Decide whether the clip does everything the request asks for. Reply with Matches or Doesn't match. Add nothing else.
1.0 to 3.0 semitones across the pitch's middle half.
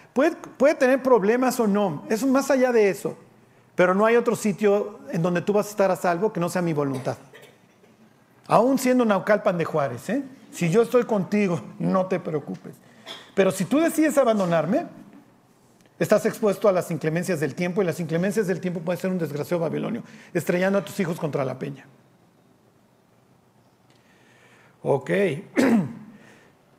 Doesn't match